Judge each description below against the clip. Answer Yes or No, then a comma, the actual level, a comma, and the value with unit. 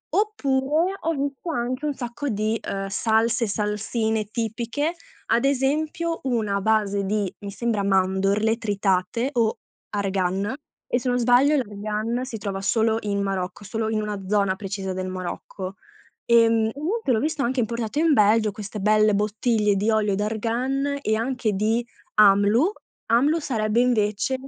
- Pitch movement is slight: No, average, 3.5 semitones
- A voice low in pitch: No, high, 220 Hz